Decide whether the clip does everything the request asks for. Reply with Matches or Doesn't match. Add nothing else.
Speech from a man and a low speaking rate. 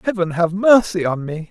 Doesn't match